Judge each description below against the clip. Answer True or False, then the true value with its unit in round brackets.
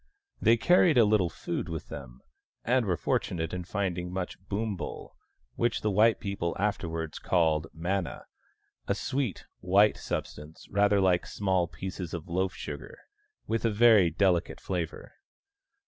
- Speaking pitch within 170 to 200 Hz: False (95 Hz)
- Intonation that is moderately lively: True (3.7 semitones)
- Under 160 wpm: True (145 wpm)